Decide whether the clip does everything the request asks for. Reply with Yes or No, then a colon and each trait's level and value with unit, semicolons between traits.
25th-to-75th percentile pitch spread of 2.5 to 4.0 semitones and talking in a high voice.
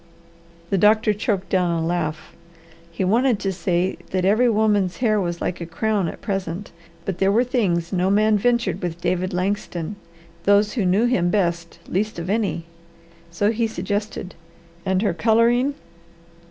Yes: average, 3.4 semitones; high, 195 Hz